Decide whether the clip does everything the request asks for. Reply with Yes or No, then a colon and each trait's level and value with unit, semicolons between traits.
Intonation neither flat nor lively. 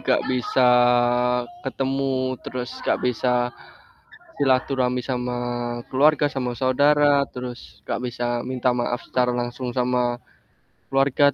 No: narrow, 1.6 semitones